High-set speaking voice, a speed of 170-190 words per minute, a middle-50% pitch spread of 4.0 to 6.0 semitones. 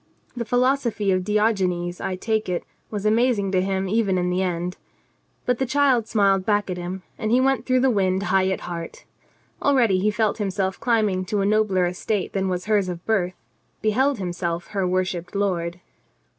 No: high, 195 Hz; average, 185 wpm; average, 3.2 semitones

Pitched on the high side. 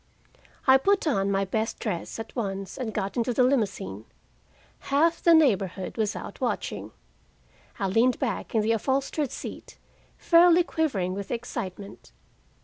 Yes: high, 225 Hz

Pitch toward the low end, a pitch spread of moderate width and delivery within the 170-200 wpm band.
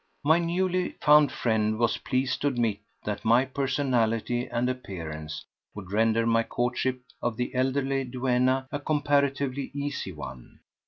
No: low, 125 Hz; average, 3.6 semitones; average, 140 wpm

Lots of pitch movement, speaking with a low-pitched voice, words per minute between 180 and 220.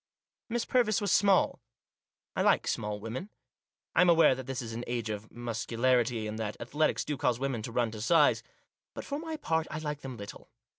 Yes: wide, 6.3 semitones; low, 130 Hz; average, 200 wpm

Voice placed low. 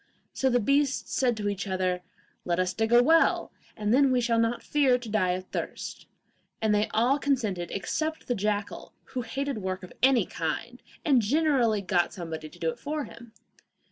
No: high, 230 Hz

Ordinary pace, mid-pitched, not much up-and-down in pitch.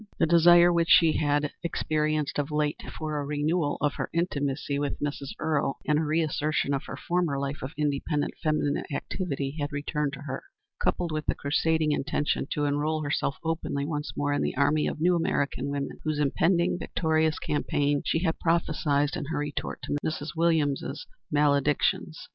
Yes: average, 170 wpm; medium, 150 Hz; narrow, 1.9 semitones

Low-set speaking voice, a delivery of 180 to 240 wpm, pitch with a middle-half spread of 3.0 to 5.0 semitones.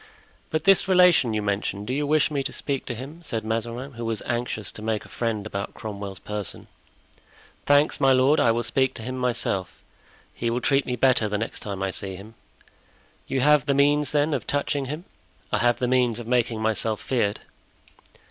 Yes: low, 120 Hz; average, 195 wpm; average, 4.2 semitones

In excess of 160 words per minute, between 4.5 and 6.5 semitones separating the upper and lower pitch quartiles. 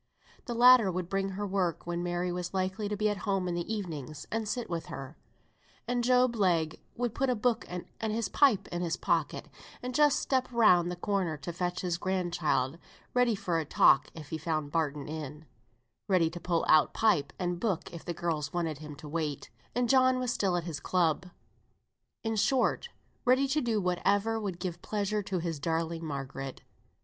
Yes: average, 195 wpm; average, 5.0 semitones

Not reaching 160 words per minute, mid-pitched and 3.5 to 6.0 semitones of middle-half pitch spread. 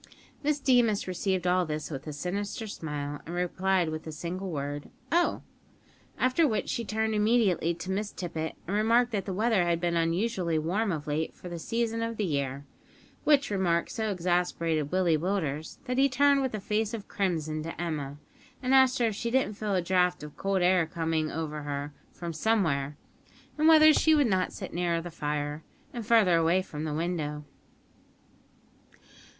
No: average, 180 wpm; medium, 180 Hz; wide, 5.5 semitones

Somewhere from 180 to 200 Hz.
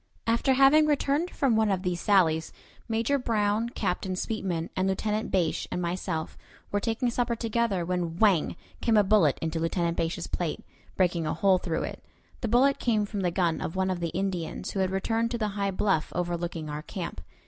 Yes: high, 190 Hz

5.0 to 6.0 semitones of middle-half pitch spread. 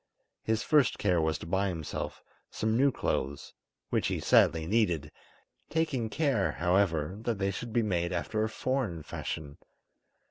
Yes: wide, 5.6 semitones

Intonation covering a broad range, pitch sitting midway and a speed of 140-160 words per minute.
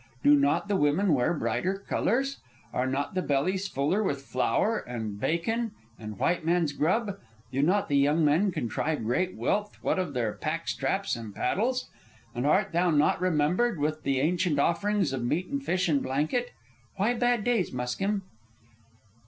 No: wide, 6.0 semitones; medium, 170 Hz; average, 170 wpm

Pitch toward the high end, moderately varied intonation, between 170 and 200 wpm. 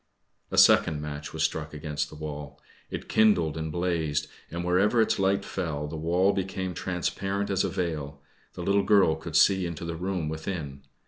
No: very low, 85 Hz; average, 3.9 semitones; average, 180 wpm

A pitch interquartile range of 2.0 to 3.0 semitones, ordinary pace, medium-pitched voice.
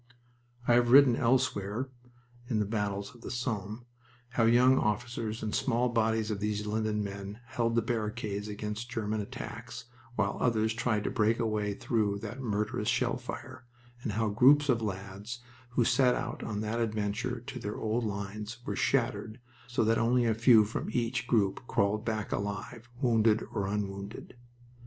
No: narrow, 2.5 semitones; average, 170 wpm; low, 110 Hz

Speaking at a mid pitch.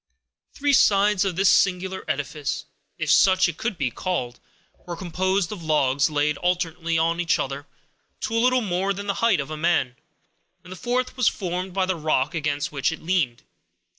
Yes: medium, 175 Hz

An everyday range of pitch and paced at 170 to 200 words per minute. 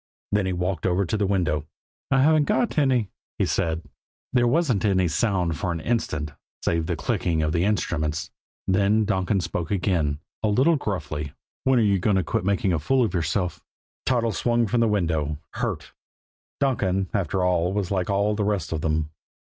Yes: average, 4.4 semitones; average, 185 wpm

